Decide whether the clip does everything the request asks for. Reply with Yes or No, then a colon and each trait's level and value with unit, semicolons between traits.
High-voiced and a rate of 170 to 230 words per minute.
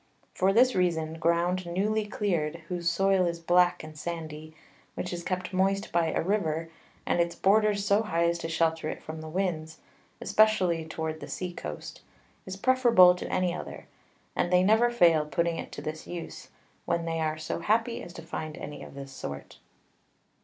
No: medium, 170 Hz; average, 180 wpm